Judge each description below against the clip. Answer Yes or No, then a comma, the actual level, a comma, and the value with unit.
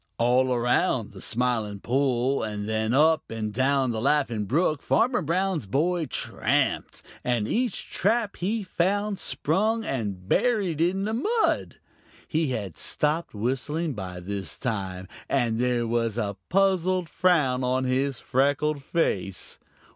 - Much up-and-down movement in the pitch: Yes, wide, 7.6 semitones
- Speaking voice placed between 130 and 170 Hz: Yes, low, 135 Hz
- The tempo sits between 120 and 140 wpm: Yes, slow, 135 wpm